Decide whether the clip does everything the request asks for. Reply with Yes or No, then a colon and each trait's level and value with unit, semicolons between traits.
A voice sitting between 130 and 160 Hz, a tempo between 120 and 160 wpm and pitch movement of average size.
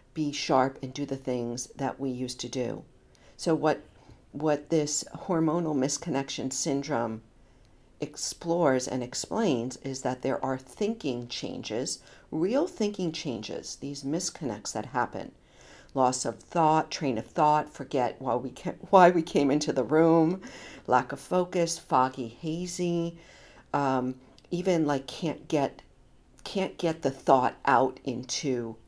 Yes: medium, 140 Hz; slow, 135 wpm; average, 4.1 semitones